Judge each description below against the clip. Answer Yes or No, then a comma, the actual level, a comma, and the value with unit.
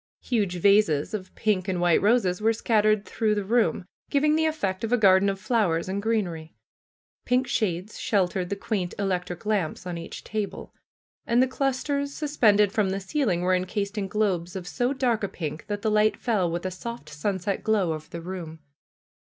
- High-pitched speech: Yes, high, 200 Hz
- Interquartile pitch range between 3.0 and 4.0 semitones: Yes, average, 3.6 semitones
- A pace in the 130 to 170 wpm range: No, average, 190 wpm